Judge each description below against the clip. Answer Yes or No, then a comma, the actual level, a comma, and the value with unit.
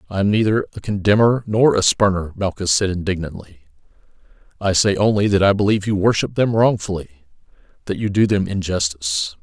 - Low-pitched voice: Yes, very low, 95 Hz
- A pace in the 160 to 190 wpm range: Yes, average, 165 wpm